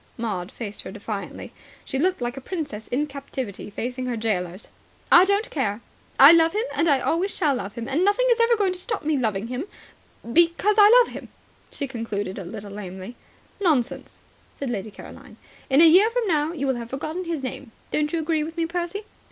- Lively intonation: Yes, wide, 7.0 semitones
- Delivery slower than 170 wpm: No, fast, 205 wpm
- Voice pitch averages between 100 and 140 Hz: No, very high, 285 Hz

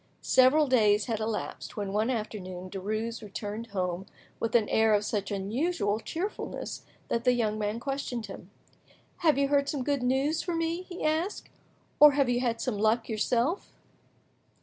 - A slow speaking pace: No, average, 165 wpm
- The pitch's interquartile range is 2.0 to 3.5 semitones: No, average, 5.0 semitones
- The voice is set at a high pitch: Yes, high, 230 Hz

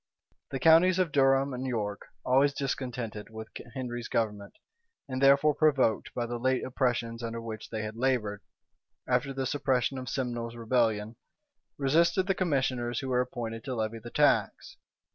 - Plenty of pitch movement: No, average, 2.8 semitones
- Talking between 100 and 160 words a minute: Yes, average, 155 wpm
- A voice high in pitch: No, low, 125 Hz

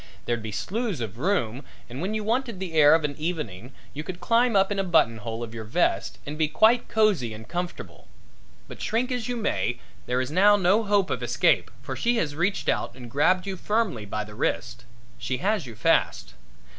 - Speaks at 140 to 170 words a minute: No, fast, 205 wpm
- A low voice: No, medium, 170 Hz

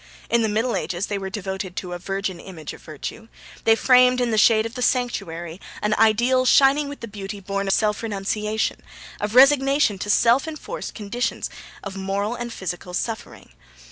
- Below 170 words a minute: No, average, 180 wpm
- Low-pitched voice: No, high, 215 Hz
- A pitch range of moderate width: Yes, average, 3.9 semitones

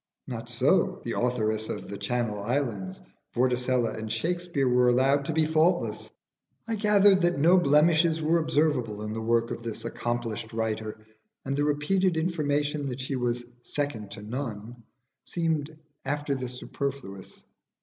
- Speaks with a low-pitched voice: Yes, low, 130 Hz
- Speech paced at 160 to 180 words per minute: No, average, 150 wpm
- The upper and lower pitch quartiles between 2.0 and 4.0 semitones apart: No, average, 5.3 semitones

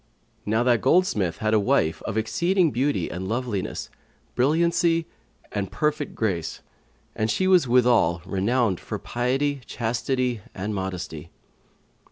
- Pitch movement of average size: No, wide, 6.0 semitones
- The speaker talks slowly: Yes, slow, 125 wpm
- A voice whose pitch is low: Yes, low, 120 Hz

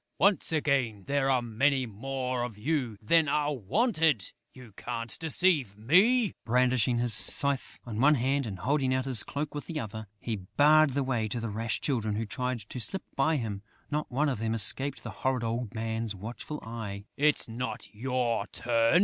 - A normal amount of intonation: Yes, average, 4.1 semitones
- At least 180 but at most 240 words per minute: Yes, average, 185 wpm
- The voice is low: Yes, low, 125 Hz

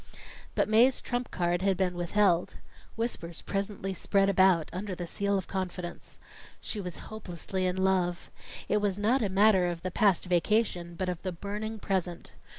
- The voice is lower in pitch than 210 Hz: Yes, high, 190 Hz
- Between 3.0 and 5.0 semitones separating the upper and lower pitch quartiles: No, narrow, 2.6 semitones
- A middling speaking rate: Yes, average, 165 wpm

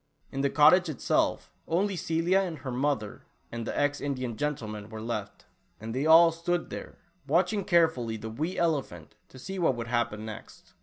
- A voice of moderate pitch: Yes, medium, 145 Hz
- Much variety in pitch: Yes, wide, 6.3 semitones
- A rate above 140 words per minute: Yes, average, 175 wpm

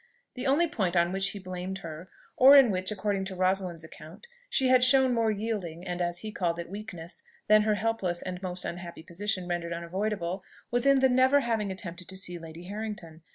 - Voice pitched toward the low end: No, high, 190 Hz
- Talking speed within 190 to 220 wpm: Yes, average, 200 wpm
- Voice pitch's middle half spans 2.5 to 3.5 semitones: No, average, 4.0 semitones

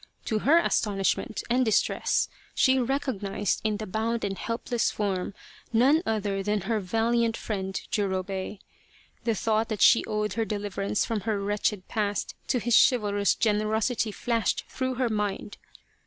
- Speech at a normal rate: Yes, average, 150 wpm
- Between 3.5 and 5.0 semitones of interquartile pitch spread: No, narrow, 2.4 semitones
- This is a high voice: Yes, high, 215 Hz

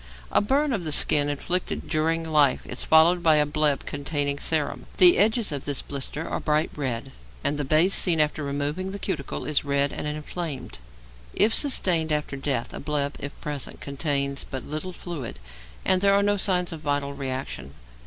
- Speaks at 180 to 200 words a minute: Yes, average, 185 wpm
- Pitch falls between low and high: Yes, medium, 150 Hz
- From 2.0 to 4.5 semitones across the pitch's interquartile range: Yes, average, 3.6 semitones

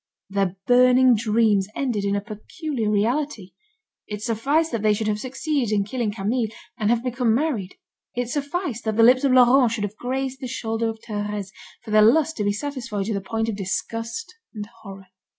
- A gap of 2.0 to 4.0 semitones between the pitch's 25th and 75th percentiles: Yes, average, 3.6 semitones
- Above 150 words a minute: Yes, average, 190 wpm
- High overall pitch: Yes, high, 225 Hz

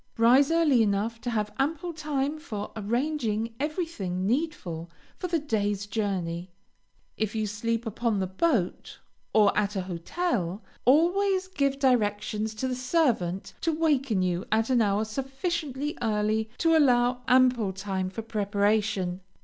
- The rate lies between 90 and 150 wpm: Yes, average, 140 wpm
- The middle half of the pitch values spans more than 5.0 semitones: Yes, wide, 5.5 semitones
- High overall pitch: Yes, high, 225 Hz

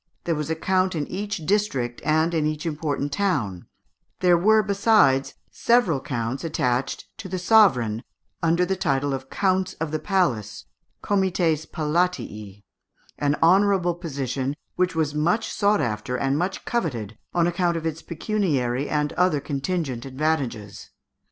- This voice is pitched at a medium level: Yes, medium, 160 Hz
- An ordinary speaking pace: Yes, average, 145 wpm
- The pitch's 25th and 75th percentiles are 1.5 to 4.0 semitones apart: No, wide, 5.4 semitones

